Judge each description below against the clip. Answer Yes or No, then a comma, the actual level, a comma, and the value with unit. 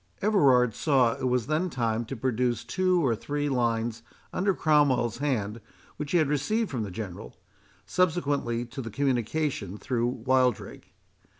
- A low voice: Yes, low, 130 Hz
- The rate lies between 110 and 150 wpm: Yes, average, 145 wpm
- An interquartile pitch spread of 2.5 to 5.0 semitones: Yes, average, 4.2 semitones